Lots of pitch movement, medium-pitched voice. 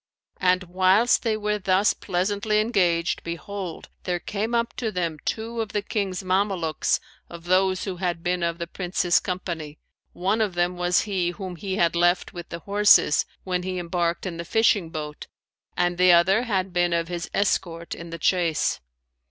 No: average, 2.7 semitones; medium, 180 Hz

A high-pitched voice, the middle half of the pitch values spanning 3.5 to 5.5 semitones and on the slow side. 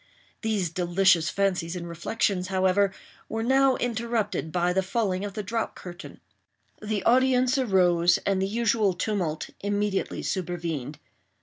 Yes: high, 195 Hz; average, 3.9 semitones; slow, 130 wpm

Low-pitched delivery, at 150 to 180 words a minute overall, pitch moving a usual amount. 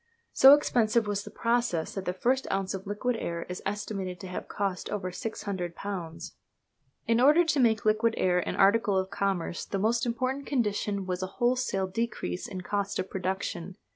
No: high, 200 Hz; average, 175 wpm; average, 3.8 semitones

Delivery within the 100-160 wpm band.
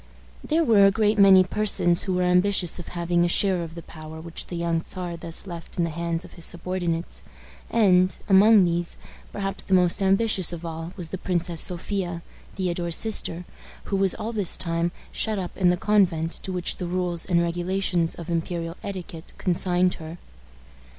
No: average, 185 wpm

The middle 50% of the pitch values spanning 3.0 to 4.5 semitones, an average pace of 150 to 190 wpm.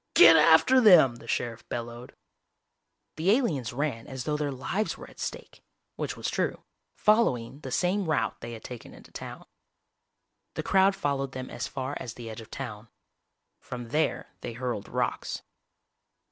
No: average, 5.3 semitones; average, 160 wpm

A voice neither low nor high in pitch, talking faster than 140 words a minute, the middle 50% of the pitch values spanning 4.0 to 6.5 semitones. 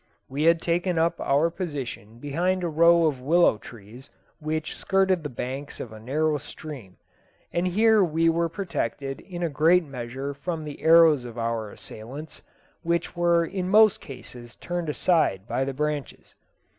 Yes: medium, 155 Hz; average, 160 wpm; average, 4.4 semitones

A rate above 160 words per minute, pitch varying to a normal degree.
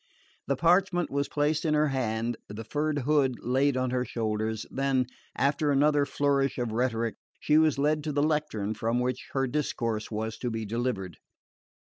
Yes: average, 170 wpm; average, 4.4 semitones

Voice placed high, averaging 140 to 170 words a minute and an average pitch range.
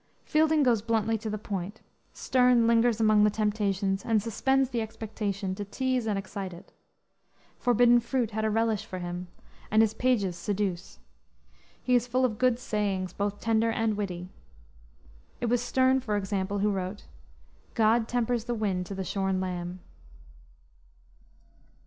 Yes: high, 215 Hz; average, 155 wpm; average, 3.3 semitones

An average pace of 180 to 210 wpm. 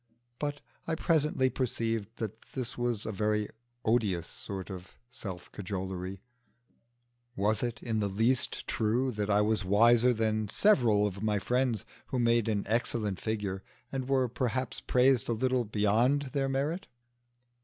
No: average, 145 wpm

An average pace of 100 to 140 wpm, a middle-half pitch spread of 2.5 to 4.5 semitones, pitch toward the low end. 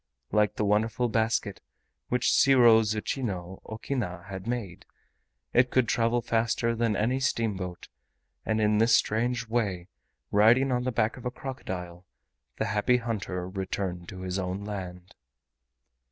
Yes: slow, 135 wpm; average, 3.9 semitones; low, 110 Hz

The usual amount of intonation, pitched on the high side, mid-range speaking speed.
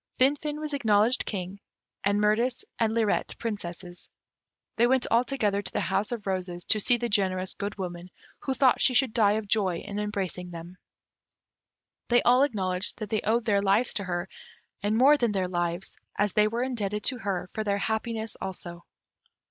Yes: average, 3.8 semitones; high, 210 Hz; average, 180 wpm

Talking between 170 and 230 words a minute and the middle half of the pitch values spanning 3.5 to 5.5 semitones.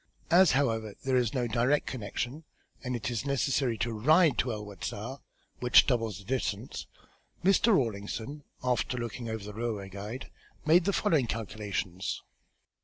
No: average, 150 wpm; average, 4.2 semitones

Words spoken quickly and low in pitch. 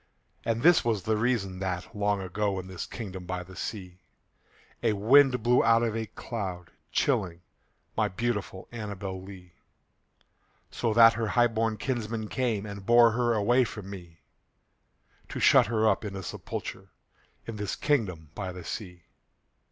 No: average, 155 wpm; low, 105 Hz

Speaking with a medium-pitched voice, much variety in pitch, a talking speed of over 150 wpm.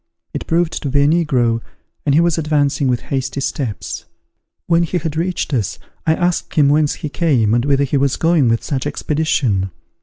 No: medium, 145 Hz; average, 3.7 semitones; average, 190 wpm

